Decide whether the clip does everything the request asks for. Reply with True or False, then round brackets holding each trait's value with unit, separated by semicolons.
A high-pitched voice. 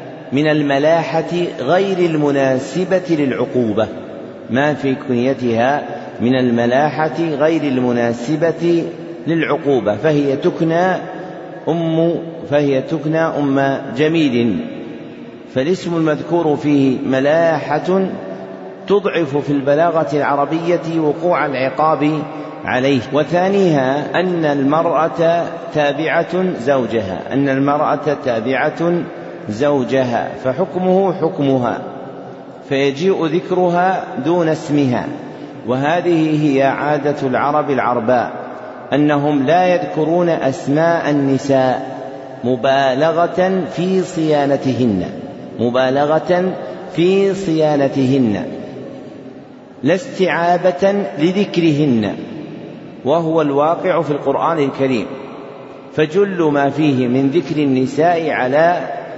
False (150 Hz)